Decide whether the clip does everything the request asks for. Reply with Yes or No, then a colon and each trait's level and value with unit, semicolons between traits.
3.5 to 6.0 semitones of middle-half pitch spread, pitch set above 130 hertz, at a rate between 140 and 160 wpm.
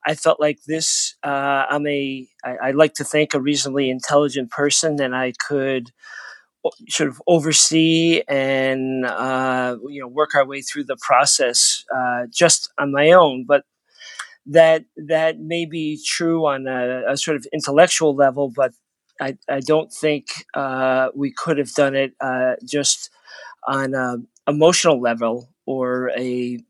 No: average, 3.0 semitones; medium, 140 Hz; average, 155 wpm